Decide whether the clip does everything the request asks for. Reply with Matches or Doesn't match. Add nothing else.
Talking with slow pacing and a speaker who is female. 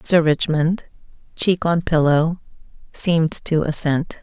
Matches